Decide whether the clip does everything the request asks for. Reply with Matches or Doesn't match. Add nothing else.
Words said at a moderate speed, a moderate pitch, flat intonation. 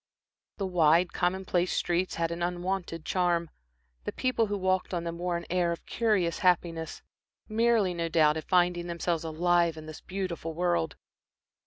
Matches